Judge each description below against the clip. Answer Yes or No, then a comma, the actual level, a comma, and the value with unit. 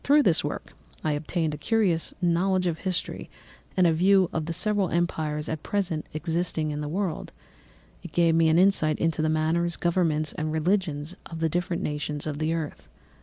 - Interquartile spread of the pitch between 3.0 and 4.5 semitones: No, narrow, 2.6 semitones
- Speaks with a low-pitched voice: No, medium, 165 Hz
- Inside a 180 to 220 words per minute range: Yes, average, 185 wpm